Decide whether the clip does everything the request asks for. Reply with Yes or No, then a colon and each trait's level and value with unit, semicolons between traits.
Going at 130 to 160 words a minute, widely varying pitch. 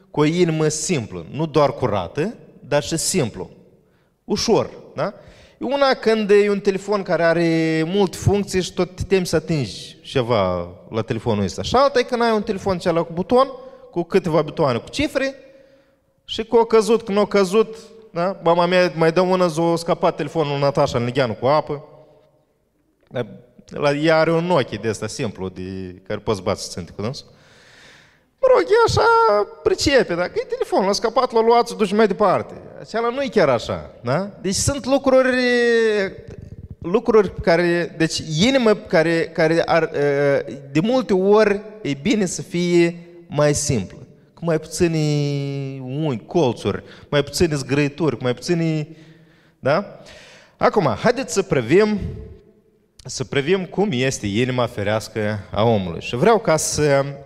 Yes: average, 155 wpm; wide, 6.9 semitones